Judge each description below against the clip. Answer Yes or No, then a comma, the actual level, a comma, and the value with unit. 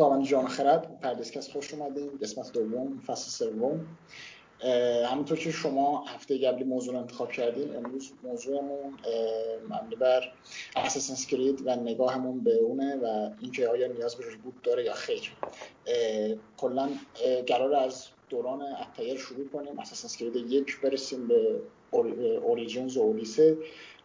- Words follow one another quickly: No, average, 130 wpm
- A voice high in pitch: No, medium, 140 Hz